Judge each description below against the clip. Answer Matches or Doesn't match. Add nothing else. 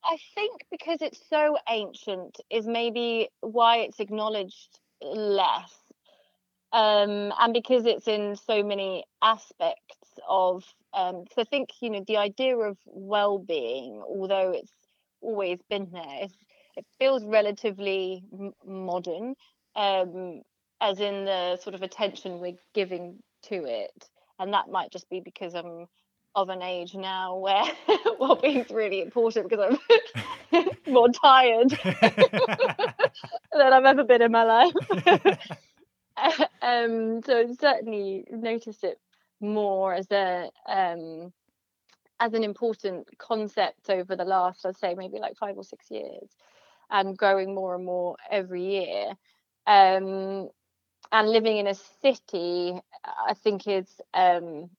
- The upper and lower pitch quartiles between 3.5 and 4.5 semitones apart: Matches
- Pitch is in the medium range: Doesn't match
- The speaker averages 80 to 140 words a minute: Matches